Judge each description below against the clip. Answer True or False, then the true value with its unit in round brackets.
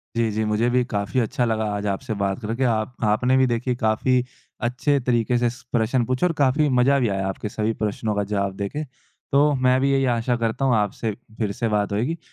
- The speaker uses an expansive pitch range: False (3.2 semitones)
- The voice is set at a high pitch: False (115 Hz)